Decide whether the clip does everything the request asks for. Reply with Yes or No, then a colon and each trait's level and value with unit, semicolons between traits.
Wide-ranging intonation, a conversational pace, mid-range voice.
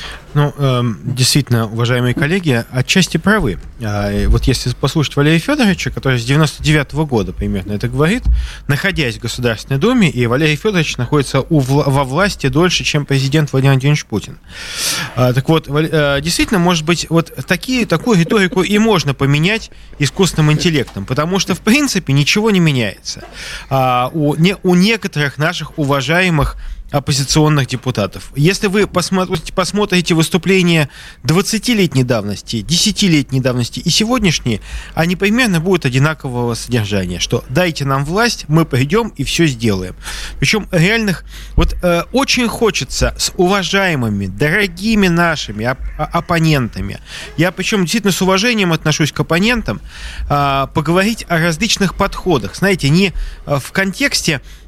Yes: wide, 6.2 semitones; average, 120 wpm; medium, 155 Hz